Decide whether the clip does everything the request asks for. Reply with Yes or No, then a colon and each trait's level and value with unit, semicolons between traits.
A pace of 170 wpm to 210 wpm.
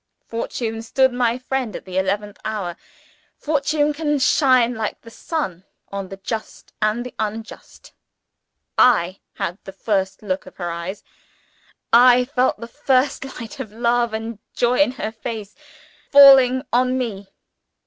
No: average, 145 wpm